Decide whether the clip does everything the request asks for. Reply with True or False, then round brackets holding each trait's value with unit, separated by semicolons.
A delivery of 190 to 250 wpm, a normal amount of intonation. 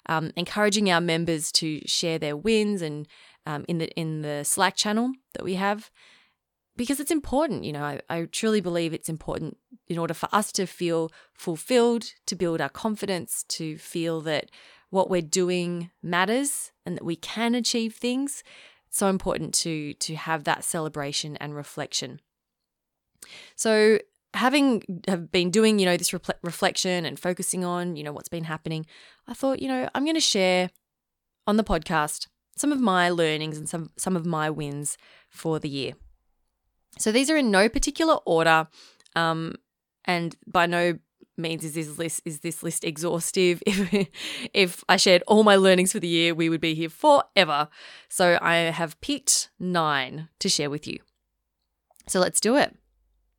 False (170 wpm; 4.4 semitones)